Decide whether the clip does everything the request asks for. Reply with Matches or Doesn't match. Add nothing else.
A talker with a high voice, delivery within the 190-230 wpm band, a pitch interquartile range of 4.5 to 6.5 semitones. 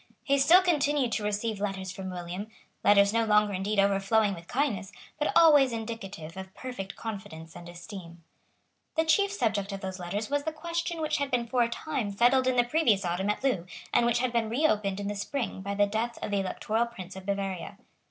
Matches